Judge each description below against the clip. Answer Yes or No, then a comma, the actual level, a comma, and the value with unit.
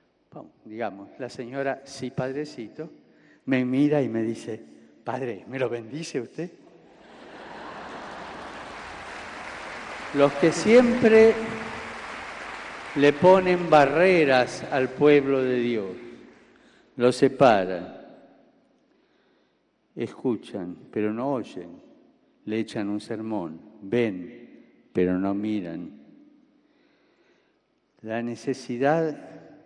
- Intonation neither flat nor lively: No, wide, 5.8 semitones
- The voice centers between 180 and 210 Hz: No, low, 135 Hz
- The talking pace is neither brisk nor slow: No, slow, 85 wpm